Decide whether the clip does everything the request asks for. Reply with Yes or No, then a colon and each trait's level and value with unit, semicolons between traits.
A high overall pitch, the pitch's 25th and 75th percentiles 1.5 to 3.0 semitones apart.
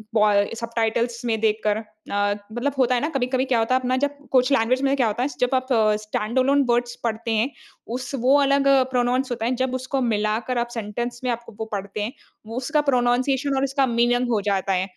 Yes: high, 245 Hz; average, 2.7 semitones